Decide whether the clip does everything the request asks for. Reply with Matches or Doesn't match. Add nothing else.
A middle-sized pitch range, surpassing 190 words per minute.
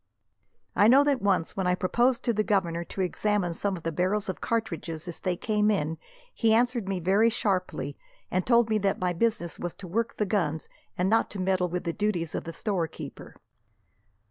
Matches